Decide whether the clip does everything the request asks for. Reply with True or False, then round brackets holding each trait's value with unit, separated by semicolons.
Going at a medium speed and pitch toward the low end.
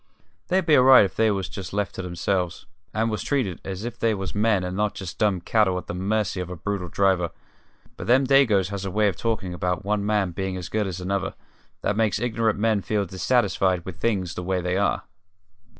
False (225 wpm; 100 Hz)